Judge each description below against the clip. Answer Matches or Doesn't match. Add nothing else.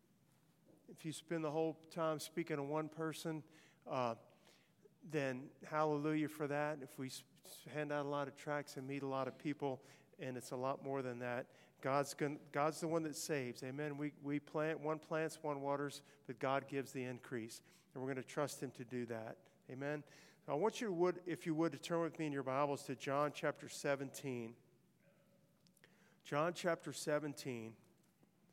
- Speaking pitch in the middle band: Matches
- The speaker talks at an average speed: Matches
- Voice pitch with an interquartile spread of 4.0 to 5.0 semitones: Doesn't match